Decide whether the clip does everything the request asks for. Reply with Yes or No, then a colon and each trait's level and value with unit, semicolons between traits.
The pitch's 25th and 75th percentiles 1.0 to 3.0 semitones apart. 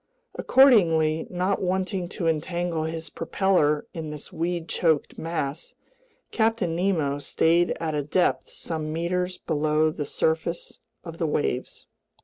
Yes: narrow, 2.6 semitones